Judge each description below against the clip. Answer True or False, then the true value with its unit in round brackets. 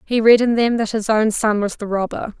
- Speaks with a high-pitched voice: True (220 Hz)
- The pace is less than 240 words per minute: False (275 wpm)